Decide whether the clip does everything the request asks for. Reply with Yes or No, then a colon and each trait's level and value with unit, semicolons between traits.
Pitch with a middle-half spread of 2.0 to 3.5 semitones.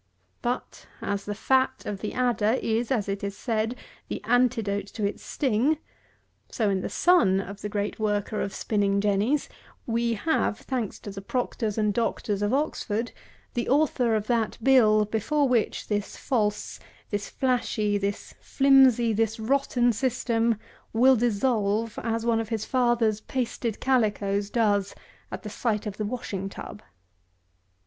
Yes: average, 3.0 semitones